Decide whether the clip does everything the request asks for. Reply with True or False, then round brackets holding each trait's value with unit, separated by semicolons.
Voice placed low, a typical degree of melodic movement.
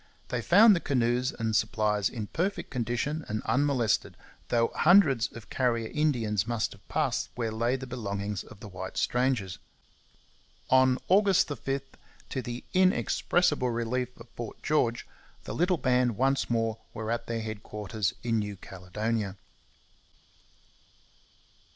True (120 Hz; 3.7 semitones)